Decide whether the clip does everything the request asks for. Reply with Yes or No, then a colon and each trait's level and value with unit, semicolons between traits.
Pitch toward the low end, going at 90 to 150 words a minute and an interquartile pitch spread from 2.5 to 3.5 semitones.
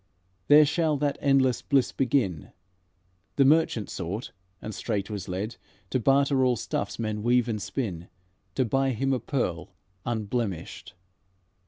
No: low, 120 Hz; average, 140 wpm; average, 4.5 semitones